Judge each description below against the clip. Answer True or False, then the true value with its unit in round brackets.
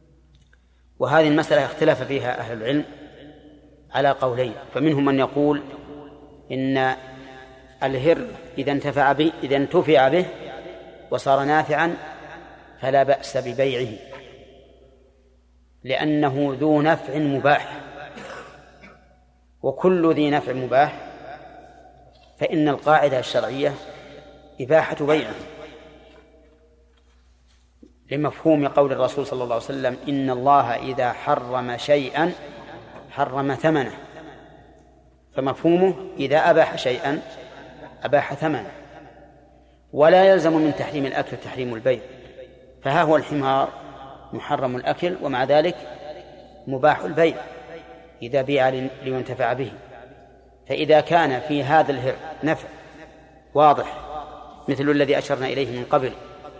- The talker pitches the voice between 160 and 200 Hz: False (140 Hz)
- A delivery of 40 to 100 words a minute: True (95 wpm)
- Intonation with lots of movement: False (2.9 semitones)